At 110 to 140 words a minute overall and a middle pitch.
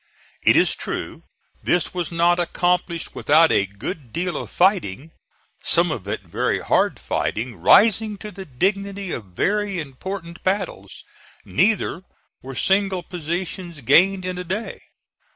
Yes: slow, 135 wpm; medium, 175 Hz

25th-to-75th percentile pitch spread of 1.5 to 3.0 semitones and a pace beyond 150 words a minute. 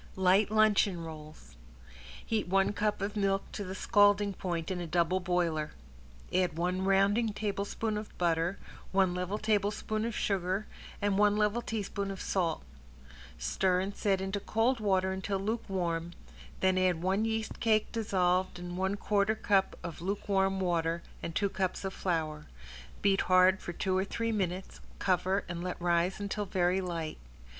Yes: narrow, 2.4 semitones; average, 160 wpm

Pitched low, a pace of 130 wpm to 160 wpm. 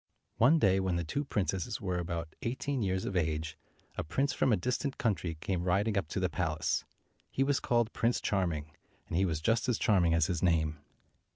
No: very low, 95 Hz; fast, 205 wpm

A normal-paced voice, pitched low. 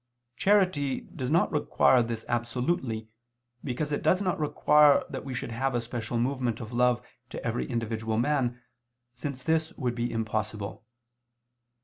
Yes: average, 145 wpm; low, 125 Hz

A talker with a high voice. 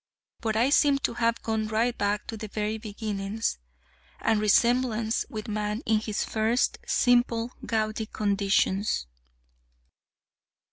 Yes: high, 220 Hz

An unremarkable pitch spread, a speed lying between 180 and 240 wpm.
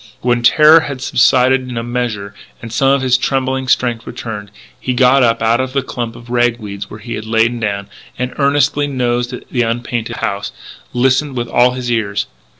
No: narrow, 2.2 semitones; average, 190 wpm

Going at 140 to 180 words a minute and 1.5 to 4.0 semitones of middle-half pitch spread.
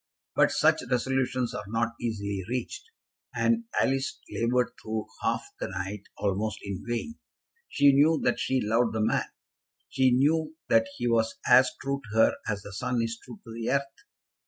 Yes: average, 170 wpm; average, 3.3 semitones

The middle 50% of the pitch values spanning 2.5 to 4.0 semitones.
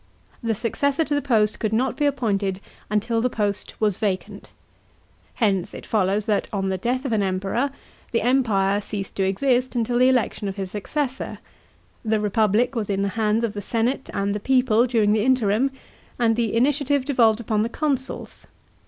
Yes: average, 3.6 semitones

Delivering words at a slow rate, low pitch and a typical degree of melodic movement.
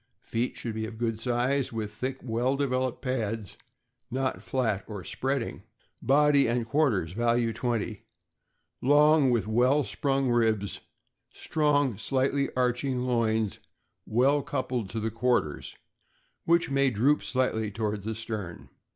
Yes: slow, 130 wpm; low, 120 Hz; average, 3.4 semitones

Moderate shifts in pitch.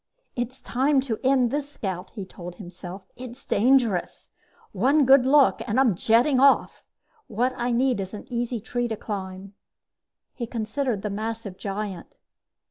Yes: average, 4.5 semitones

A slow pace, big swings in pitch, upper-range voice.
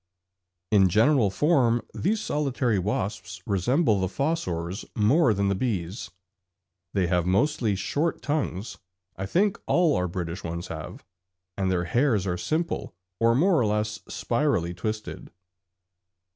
No: slow, 130 wpm; wide, 7.2 semitones; low, 105 Hz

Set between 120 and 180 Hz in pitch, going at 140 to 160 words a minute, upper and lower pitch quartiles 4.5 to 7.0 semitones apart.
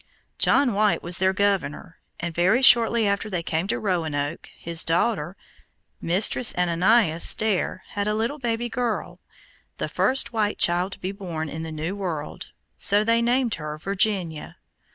No: high, 195 Hz; average, 155 wpm; average, 4.8 semitones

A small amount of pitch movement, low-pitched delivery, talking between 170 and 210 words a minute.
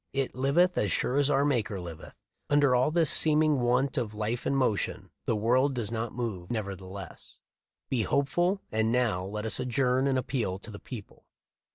No: average, 4.5 semitones; low, 125 Hz; average, 175 wpm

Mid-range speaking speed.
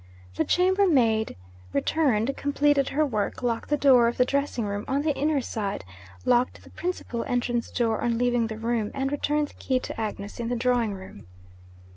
Yes: average, 180 wpm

